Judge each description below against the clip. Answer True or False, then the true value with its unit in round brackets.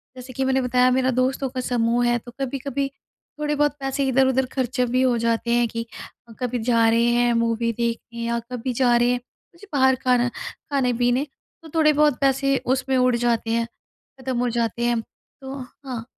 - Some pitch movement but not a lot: False (1.9 semitones)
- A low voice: False (250 Hz)